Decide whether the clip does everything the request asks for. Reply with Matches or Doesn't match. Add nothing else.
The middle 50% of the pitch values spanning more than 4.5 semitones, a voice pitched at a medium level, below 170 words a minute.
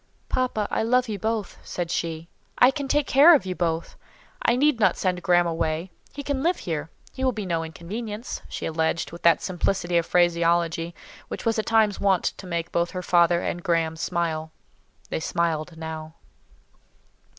Doesn't match